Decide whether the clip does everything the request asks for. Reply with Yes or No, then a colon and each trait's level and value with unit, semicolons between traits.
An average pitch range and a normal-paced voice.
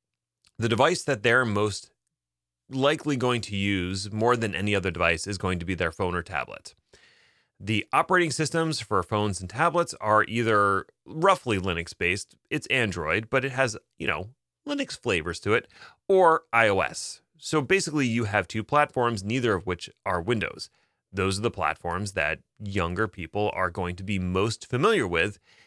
No: wide, 5.8 semitones; average, 170 wpm